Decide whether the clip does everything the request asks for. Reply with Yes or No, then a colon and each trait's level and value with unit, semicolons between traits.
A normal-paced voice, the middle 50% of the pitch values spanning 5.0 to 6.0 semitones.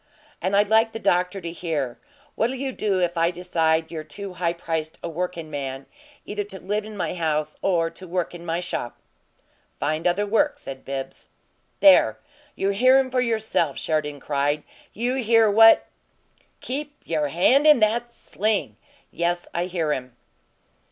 Yes: average, 165 wpm; average, 5.3 semitones